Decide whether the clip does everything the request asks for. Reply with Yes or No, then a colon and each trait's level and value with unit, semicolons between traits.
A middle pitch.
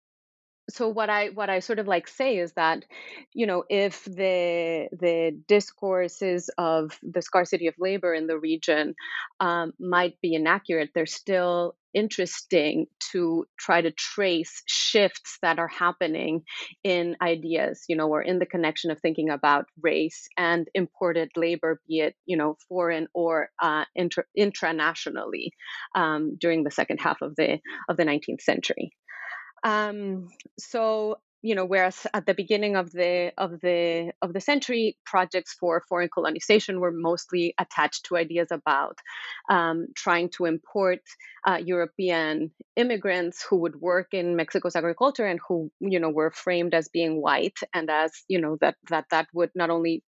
Yes: medium, 175 Hz